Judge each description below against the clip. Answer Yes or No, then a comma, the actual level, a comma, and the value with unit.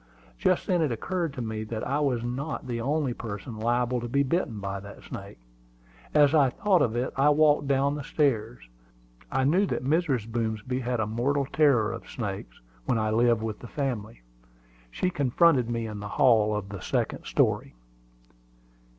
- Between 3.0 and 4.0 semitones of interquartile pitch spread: No, average, 4.4 semitones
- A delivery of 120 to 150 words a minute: No, average, 180 wpm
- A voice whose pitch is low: Yes, low, 120 Hz